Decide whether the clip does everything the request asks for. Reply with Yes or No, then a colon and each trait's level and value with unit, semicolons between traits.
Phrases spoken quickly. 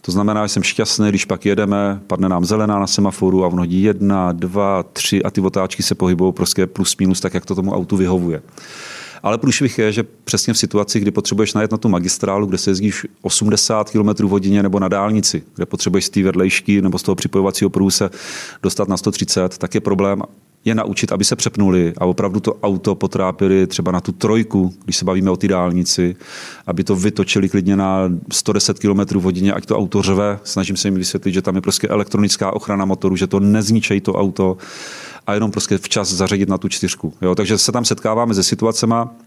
Yes: fast, 205 wpm